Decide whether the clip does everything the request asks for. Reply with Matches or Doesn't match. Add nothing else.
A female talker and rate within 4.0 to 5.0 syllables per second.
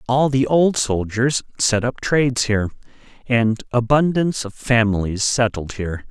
Doesn't match